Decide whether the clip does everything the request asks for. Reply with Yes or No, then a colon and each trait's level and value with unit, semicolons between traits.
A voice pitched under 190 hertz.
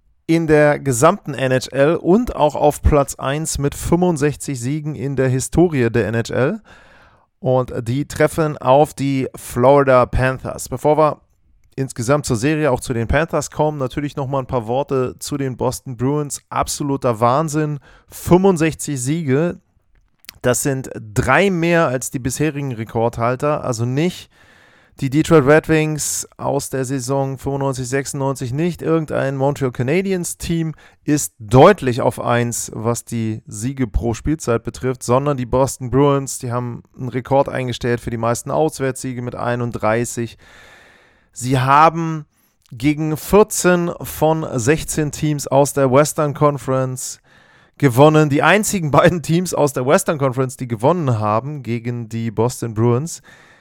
Yes: low, 135 Hz